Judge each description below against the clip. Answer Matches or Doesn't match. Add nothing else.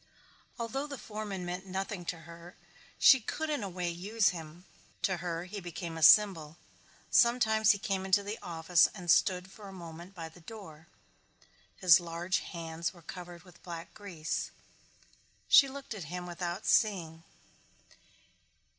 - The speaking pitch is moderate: Matches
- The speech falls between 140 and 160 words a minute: Matches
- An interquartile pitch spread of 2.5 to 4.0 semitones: Matches